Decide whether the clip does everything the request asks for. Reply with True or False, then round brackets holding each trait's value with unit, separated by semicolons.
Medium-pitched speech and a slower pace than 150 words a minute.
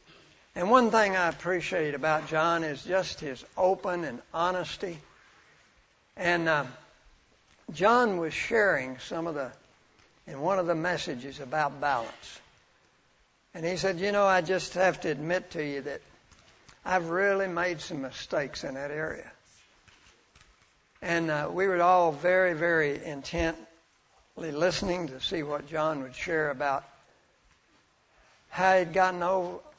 True (170 Hz; 140 wpm)